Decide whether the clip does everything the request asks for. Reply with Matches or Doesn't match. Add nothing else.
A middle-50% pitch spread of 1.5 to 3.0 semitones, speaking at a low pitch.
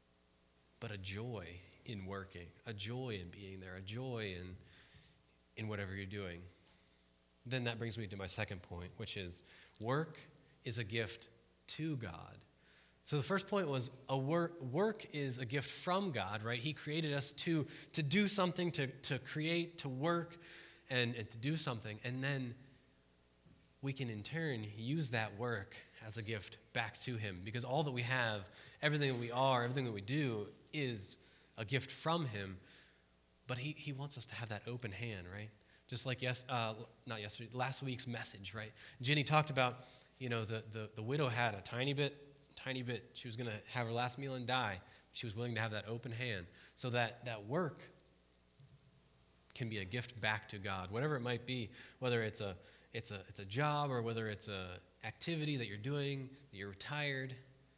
Doesn't match